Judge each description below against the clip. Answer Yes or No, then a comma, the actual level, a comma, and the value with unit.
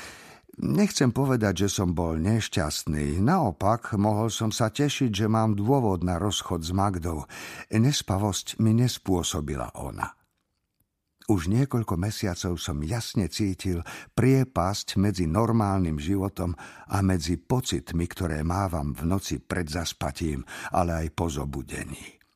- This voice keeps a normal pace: Yes, average, 120 wpm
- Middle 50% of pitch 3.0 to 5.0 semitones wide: Yes, average, 4.3 semitones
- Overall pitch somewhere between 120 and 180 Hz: No, very low, 95 Hz